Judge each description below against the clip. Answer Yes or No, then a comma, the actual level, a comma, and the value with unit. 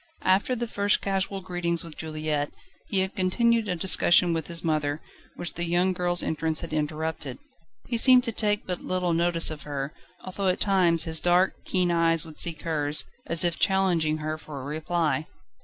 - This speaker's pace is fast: No, average, 185 wpm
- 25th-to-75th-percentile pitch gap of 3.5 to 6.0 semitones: No, average, 3.1 semitones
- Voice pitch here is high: No, medium, 170 Hz